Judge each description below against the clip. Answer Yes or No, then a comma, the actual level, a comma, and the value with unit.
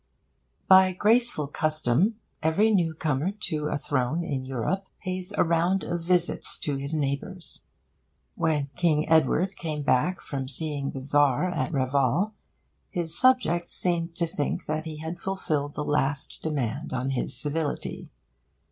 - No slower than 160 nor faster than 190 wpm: No, average, 140 wpm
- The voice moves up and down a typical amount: Yes, average, 4.0 semitones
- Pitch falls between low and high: Yes, medium, 155 Hz